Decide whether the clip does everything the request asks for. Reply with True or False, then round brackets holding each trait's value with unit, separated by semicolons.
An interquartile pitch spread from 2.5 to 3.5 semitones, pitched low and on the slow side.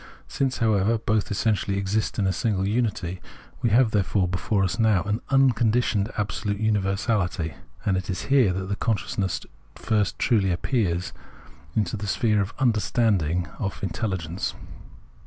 True (2.8 semitones; 105 Hz; 130 wpm)